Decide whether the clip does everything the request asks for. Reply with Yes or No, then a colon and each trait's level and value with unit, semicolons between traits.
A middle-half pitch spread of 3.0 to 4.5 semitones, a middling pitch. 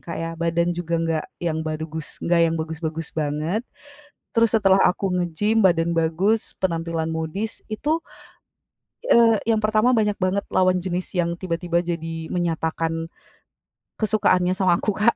Yes: average, 3.6 semitones; medium, 175 Hz